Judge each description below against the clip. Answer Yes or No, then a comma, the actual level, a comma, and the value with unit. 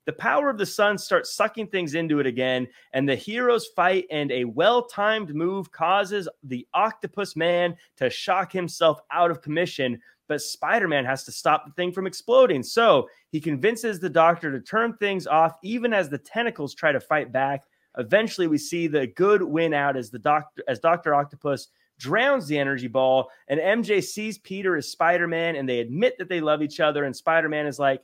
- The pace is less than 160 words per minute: No, average, 195 wpm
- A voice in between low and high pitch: Yes, medium, 165 Hz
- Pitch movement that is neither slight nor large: No, wide, 5.8 semitones